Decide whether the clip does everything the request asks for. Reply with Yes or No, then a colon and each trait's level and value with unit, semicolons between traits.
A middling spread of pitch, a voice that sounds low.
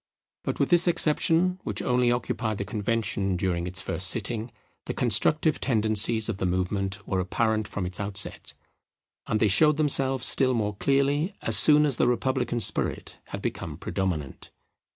No: wide, 5.7 semitones; low, 110 Hz